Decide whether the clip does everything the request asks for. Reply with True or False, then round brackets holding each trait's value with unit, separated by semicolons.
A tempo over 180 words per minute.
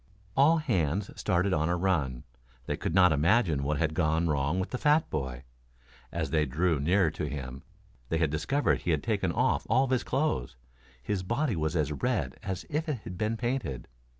True (190 wpm)